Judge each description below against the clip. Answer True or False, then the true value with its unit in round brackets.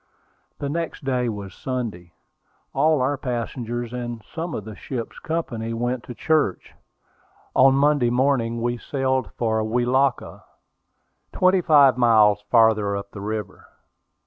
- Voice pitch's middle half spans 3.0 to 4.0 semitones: True (3.4 semitones)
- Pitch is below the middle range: True (120 Hz)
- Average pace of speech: False (130 wpm)